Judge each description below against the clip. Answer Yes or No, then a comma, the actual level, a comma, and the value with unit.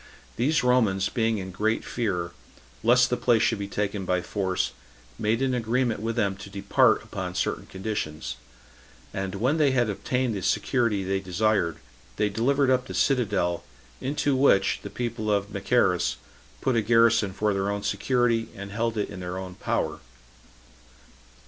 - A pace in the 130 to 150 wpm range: No, average, 160 wpm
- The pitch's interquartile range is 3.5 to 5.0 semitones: Yes, average, 3.9 semitones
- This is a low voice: Yes, low, 105 Hz